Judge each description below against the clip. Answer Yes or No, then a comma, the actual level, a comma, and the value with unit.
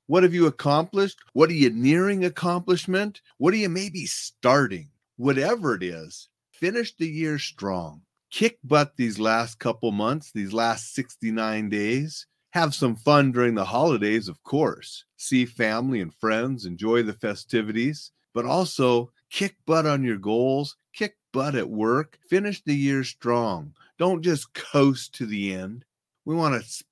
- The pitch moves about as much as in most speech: No, wide, 6.0 semitones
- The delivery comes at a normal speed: Yes, average, 160 wpm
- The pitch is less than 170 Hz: Yes, low, 135 Hz